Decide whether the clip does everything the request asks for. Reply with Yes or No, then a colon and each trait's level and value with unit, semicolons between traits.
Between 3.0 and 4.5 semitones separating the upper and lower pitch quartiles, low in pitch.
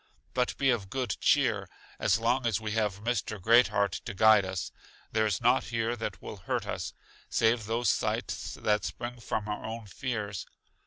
No: narrow, 2.6 semitones; low, 110 Hz